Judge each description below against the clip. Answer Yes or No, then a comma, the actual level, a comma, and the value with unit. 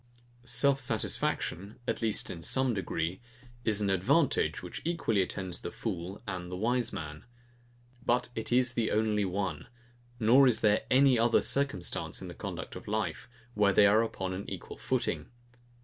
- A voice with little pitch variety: No, average, 4.3 semitones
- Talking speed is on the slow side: No, average, 165 wpm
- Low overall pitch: Yes, low, 105 Hz